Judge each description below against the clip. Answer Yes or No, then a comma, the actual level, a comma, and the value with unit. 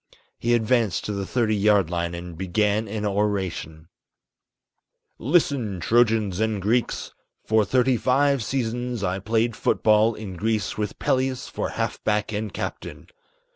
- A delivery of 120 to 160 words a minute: Yes, average, 140 wpm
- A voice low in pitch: Yes, low, 110 Hz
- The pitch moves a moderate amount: Yes, average, 3.0 semitones